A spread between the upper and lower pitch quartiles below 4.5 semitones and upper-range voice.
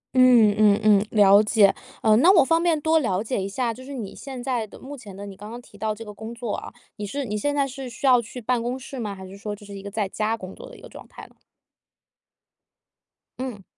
Yes: average, 3.9 semitones; high, 225 Hz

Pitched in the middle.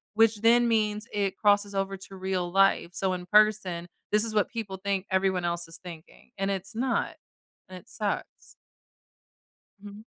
No: high, 195 Hz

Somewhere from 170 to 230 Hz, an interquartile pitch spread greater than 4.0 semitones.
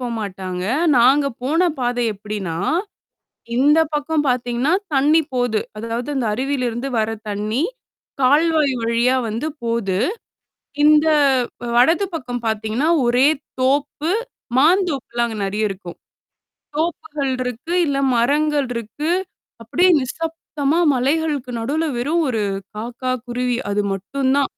No: very high, 255 Hz; average, 4.4 semitones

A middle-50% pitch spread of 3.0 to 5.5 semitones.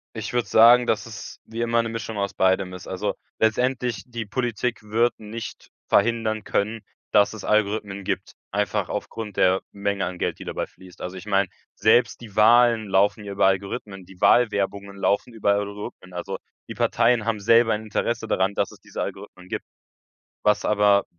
No: narrow, 2.5 semitones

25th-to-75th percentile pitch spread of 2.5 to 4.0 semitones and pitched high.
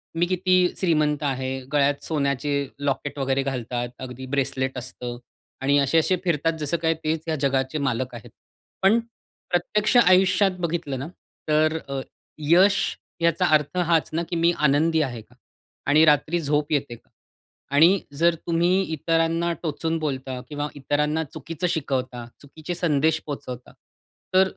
No: average, 3.6 semitones; medium, 150 Hz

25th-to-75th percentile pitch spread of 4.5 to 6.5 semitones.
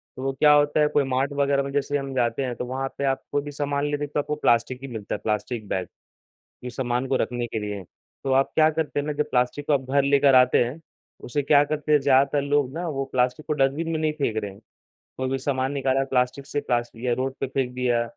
No: narrow, 2.5 semitones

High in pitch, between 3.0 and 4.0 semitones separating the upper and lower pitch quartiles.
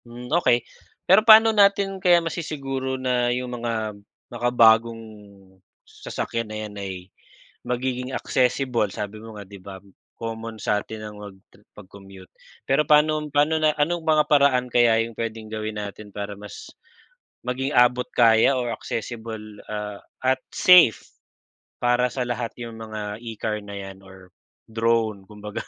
No: low, 115 Hz; average, 3.7 semitones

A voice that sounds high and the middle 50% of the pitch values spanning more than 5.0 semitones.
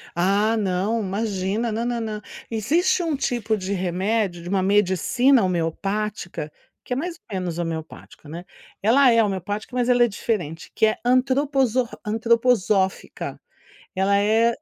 No: high, 215 Hz; average, 4.1 semitones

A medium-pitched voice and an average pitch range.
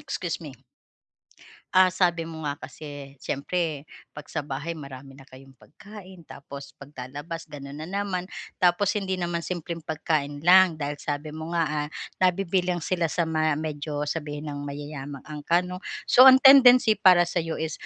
Yes: medium, 160 Hz; average, 3.7 semitones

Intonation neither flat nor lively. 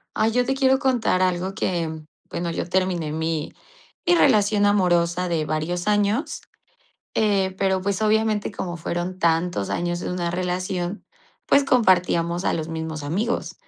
Yes: average, 3.4 semitones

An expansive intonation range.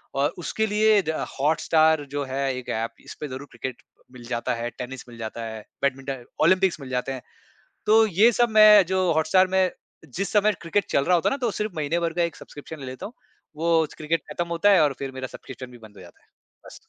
Yes: wide, 6.1 semitones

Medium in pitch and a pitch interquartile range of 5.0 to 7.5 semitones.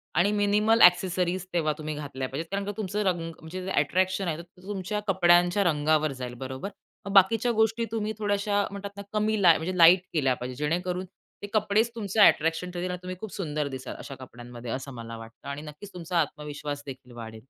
Yes: medium, 175 Hz; wide, 5.4 semitones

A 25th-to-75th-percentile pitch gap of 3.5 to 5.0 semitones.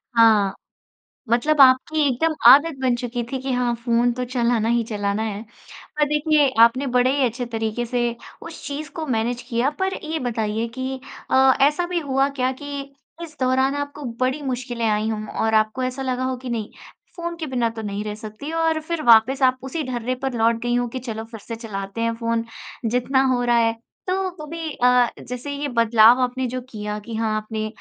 No: average, 3.1 semitones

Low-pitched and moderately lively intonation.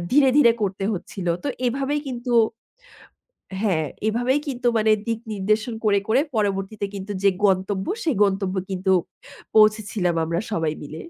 No: high, 210 Hz; average, 3.7 semitones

